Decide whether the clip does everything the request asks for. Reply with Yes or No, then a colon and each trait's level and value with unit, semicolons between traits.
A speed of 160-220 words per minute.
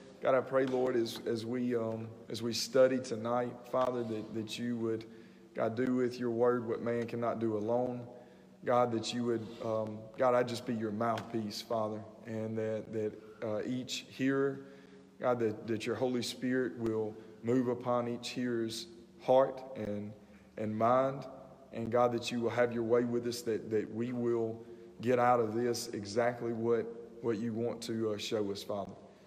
Yes: average, 180 wpm